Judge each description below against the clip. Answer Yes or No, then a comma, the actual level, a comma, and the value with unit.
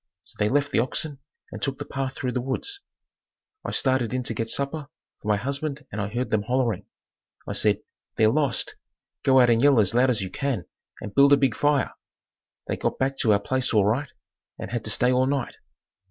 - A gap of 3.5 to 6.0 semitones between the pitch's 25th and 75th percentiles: Yes, average, 3.9 semitones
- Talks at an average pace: No, fast, 215 wpm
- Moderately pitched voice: No, low, 130 Hz